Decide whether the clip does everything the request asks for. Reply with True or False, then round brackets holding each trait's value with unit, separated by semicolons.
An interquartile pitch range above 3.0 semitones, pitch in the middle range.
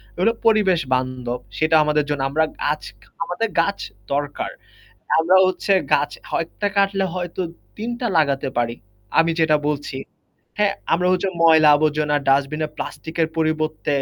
True (3.6 semitones; 155 Hz)